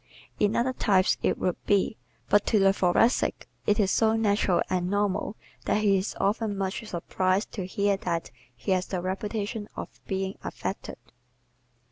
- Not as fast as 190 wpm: Yes, average, 160 wpm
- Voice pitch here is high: Yes, high, 200 Hz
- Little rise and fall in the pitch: Yes, narrow, 1.9 semitones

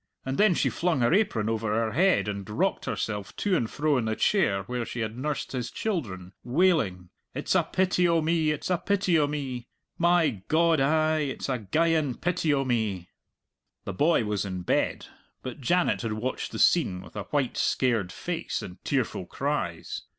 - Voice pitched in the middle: No, low, 130 Hz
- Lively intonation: Yes, wide, 7.2 semitones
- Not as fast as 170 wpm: No, average, 185 wpm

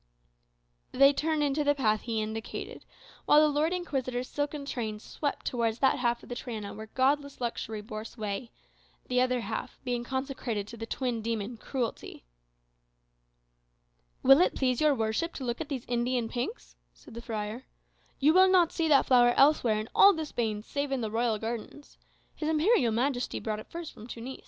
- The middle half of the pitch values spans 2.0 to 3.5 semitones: No, average, 4.2 semitones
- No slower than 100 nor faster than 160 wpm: No, average, 180 wpm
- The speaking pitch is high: Yes, high, 245 Hz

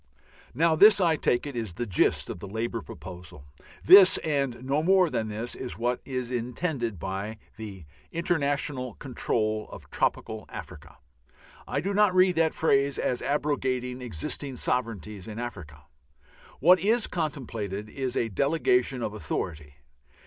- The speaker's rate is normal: Yes, average, 145 wpm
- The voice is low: Yes, low, 125 Hz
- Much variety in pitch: Yes, wide, 5.7 semitones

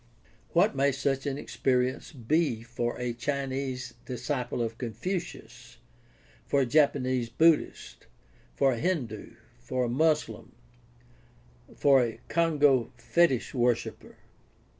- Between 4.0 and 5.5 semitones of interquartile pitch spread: No, average, 3.1 semitones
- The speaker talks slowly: Yes, slow, 110 wpm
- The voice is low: Yes, low, 130 Hz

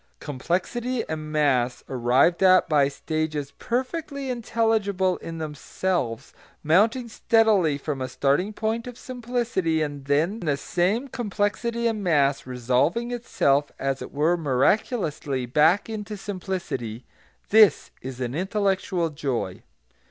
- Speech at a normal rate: No, slow, 115 wpm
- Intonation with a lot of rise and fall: Yes, wide, 7.5 semitones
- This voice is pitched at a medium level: Yes, medium, 175 Hz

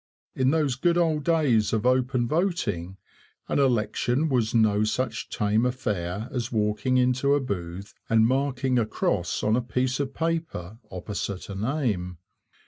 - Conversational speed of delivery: Yes, average, 150 wpm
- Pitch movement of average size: Yes, average, 4.3 semitones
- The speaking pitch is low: Yes, low, 120 Hz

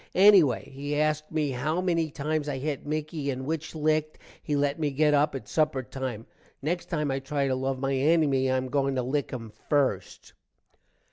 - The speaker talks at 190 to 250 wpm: Yes, average, 200 wpm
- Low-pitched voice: No, medium, 145 Hz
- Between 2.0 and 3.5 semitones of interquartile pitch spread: Yes, narrow, 2.4 semitones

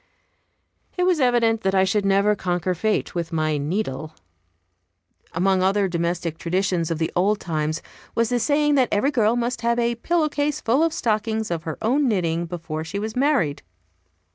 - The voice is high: Yes, high, 200 Hz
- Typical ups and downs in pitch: No, wide, 5.9 semitones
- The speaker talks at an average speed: Yes, average, 175 wpm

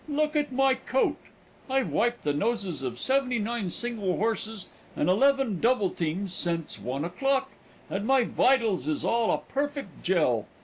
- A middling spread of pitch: No, wide, 6.8 semitones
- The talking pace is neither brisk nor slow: Yes, average, 160 wpm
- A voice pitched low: No, high, 225 Hz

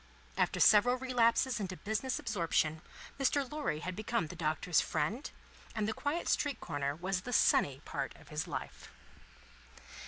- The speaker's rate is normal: Yes, average, 150 wpm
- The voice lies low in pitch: No, high, 205 Hz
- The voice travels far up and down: Yes, wide, 7.9 semitones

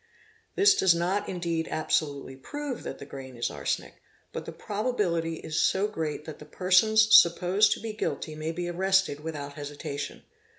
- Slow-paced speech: No, average, 165 wpm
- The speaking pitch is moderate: Yes, medium, 170 Hz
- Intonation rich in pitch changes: No, average, 5.0 semitones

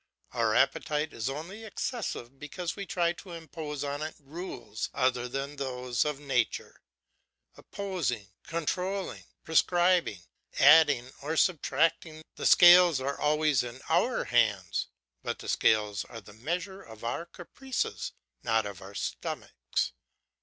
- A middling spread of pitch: No, wide, 5.8 semitones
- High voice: No, medium, 150 Hz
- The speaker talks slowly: Yes, slow, 130 wpm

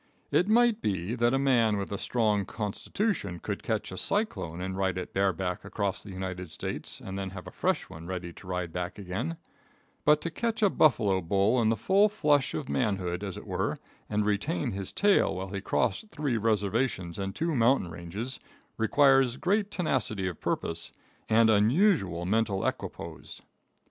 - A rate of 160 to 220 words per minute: Yes, average, 175 wpm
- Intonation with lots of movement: Yes, wide, 6.3 semitones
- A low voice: Yes, low, 105 Hz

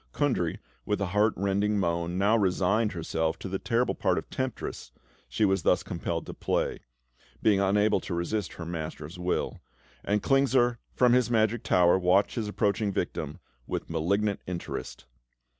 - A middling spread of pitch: Yes, average, 3.7 semitones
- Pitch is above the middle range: No, low, 100 Hz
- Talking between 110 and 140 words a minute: No, average, 160 wpm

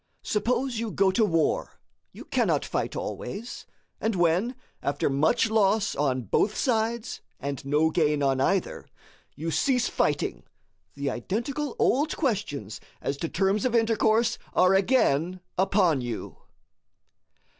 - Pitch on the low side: No, high, 195 Hz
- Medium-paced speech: No, slow, 130 wpm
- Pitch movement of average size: No, wide, 7.3 semitones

